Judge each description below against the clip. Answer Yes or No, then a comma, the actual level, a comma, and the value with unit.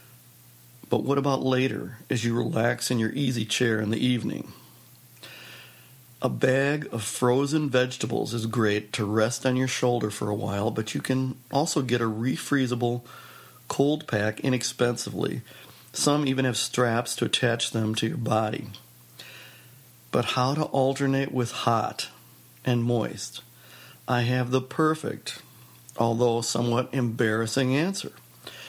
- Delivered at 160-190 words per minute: No, slow, 135 wpm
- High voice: No, low, 125 Hz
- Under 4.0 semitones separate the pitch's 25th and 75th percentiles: Yes, average, 2.8 semitones